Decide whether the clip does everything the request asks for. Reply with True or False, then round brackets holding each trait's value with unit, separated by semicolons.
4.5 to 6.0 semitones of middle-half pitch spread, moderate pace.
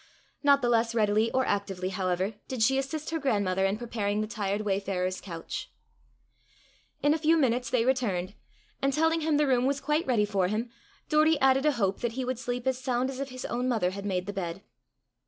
False (5.1 semitones; 210 wpm)